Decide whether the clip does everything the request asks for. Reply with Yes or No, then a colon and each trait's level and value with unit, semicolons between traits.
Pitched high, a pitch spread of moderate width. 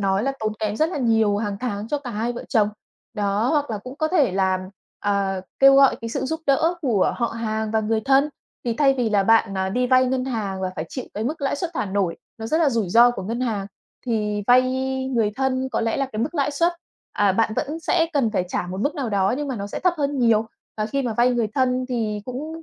Yes: high, 235 Hz; average, 4.6 semitones